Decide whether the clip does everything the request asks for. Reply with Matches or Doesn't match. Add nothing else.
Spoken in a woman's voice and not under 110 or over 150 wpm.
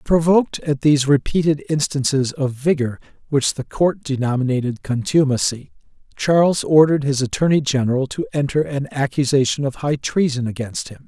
Doesn't match